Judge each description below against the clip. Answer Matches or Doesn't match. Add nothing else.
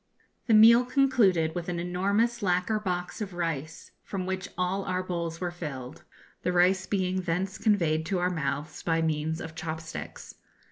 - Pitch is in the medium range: Matches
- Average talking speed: Matches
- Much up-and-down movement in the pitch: Doesn't match